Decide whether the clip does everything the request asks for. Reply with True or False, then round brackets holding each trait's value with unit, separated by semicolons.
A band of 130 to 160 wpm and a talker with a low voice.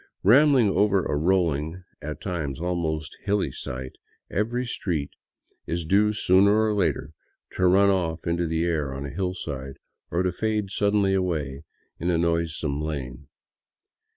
True (145 wpm; 85 Hz)